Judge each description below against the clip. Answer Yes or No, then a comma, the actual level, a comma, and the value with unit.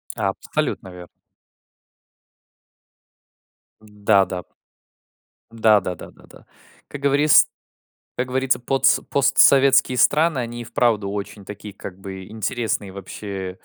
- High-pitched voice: No, low, 110 Hz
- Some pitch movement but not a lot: Yes, average, 4.7 semitones